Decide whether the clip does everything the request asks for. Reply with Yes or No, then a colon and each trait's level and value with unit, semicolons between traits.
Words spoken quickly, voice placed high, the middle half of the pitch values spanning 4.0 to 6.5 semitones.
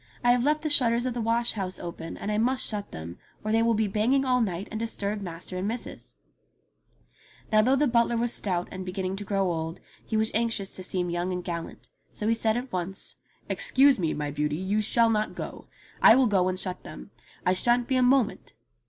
Yes: fast, 225 wpm; high, 215 Hz; average, 4.4 semitones